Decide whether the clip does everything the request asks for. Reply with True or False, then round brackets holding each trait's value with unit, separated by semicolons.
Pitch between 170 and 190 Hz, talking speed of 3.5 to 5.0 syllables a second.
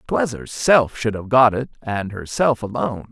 False (115 Hz; 4.6 syllables/s)